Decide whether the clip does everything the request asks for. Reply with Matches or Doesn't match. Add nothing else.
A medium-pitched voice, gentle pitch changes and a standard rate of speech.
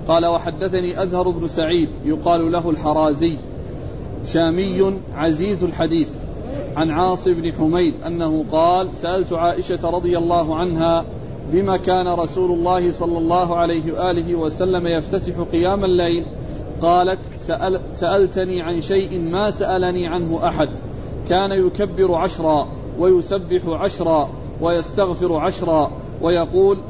Matches